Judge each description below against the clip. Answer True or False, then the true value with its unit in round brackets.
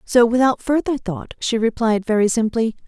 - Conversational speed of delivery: True (165 wpm)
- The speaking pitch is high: True (230 Hz)